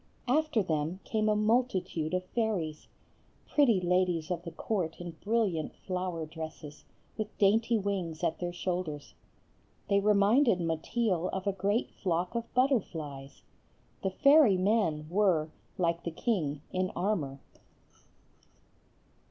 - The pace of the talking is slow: Yes, slow, 125 wpm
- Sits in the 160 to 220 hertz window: Yes, medium, 185 Hz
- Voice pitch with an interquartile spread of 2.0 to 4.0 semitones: No, average, 4.6 semitones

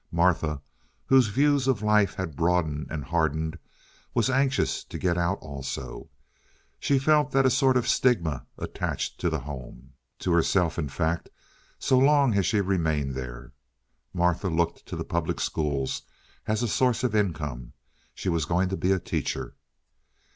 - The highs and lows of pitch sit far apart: Yes, wide, 6.5 semitones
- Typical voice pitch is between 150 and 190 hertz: No, very low, 85 Hz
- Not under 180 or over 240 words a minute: No, average, 155 wpm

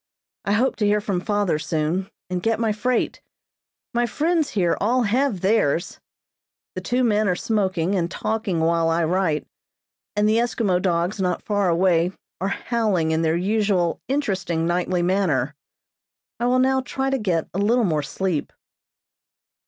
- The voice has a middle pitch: No, high, 195 Hz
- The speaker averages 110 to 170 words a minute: Yes, average, 160 wpm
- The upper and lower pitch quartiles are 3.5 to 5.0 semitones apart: Yes, average, 4.4 semitones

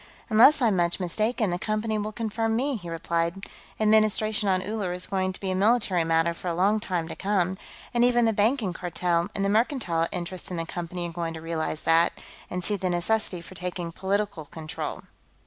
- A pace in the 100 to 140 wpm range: No, average, 200 wpm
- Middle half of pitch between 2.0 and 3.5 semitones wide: No, average, 4.0 semitones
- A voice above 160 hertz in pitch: Yes, medium, 185 Hz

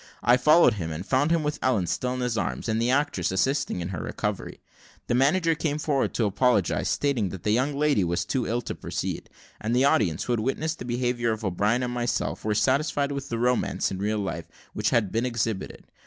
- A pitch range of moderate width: Yes, average, 4.7 semitones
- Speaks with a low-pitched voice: Yes, low, 120 Hz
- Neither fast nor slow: No, fast, 220 wpm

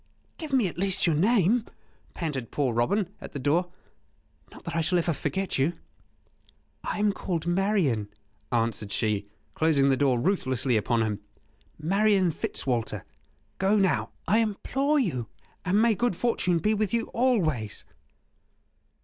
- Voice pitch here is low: No, medium, 175 Hz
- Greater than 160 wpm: No, average, 145 wpm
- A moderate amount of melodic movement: No, wide, 7.8 semitones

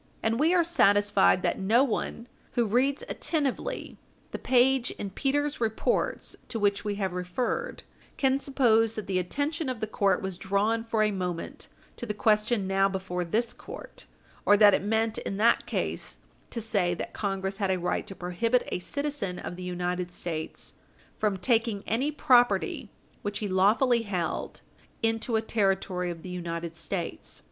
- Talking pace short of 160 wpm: No, average, 170 wpm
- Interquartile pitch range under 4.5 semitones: Yes, average, 4.1 semitones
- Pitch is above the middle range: Yes, high, 210 Hz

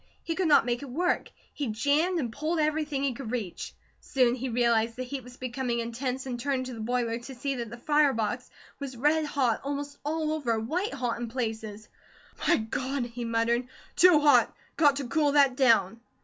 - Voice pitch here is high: Yes, very high, 255 Hz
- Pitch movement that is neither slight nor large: Yes, average, 3.6 semitones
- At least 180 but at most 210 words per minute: Yes, average, 200 wpm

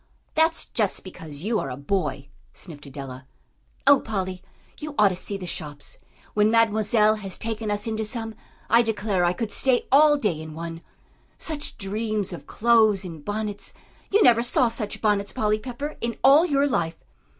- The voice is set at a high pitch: Yes, high, 210 Hz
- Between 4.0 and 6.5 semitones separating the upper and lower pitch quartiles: Yes, average, 4.4 semitones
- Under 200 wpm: Yes, average, 170 wpm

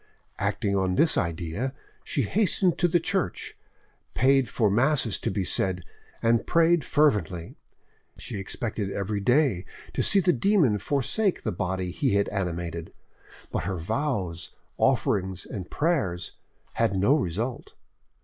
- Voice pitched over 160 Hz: No, low, 105 Hz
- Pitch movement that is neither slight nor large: No, wide, 7.9 semitones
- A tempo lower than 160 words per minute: Yes, slow, 135 wpm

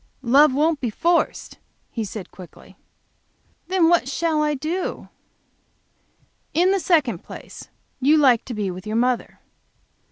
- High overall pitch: Yes, very high, 280 Hz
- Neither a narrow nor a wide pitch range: No, wide, 6.1 semitones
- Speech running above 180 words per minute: No, slow, 135 wpm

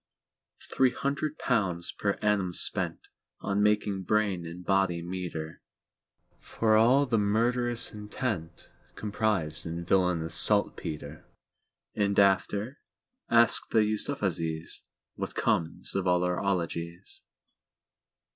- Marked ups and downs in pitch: No, average, 4.0 semitones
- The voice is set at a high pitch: No, low, 100 Hz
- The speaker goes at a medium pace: No, slow, 85 wpm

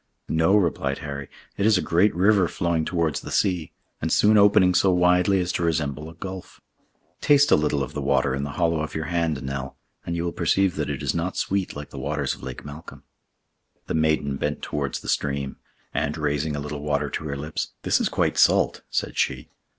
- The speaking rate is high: Yes, fast, 210 wpm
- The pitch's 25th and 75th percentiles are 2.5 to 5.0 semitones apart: Yes, average, 3.7 semitones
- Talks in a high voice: No, very low, 80 Hz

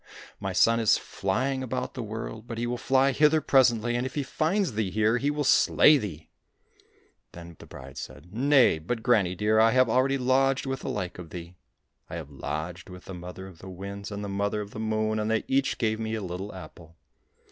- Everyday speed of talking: No, fast, 225 wpm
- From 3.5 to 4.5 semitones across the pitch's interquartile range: No, wide, 5.6 semitones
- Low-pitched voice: Yes, low, 110 Hz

